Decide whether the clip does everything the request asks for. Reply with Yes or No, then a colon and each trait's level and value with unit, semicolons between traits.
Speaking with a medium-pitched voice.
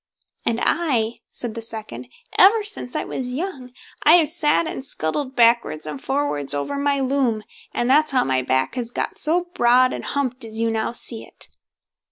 No: very high, 250 Hz